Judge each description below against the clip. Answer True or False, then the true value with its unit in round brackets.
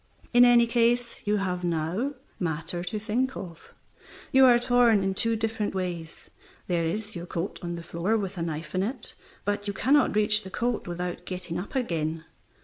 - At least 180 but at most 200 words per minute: True (185 wpm)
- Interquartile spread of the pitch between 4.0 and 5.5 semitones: True (5.1 semitones)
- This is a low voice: False (195 Hz)